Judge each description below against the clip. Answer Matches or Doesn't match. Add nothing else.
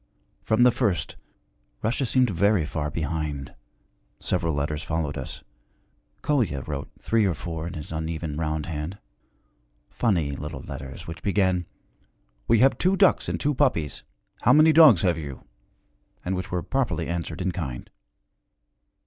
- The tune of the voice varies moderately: Doesn't match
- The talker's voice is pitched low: Matches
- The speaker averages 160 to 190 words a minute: Doesn't match